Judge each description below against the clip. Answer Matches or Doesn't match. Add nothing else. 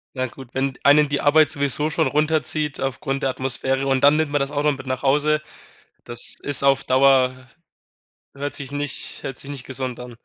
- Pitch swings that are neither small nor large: Doesn't match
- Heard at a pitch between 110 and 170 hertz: Matches